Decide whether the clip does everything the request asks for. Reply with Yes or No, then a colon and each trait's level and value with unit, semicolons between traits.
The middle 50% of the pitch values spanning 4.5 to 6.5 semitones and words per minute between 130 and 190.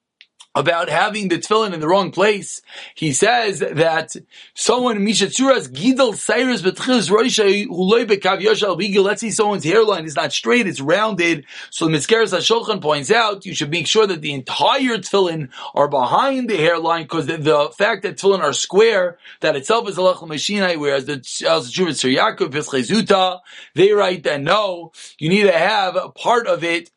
Yes: average, 4.9 semitones; average, 145 wpm